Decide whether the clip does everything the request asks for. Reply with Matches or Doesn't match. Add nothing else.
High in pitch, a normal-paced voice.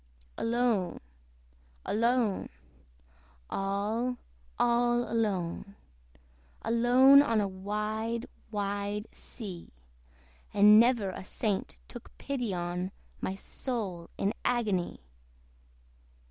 Doesn't match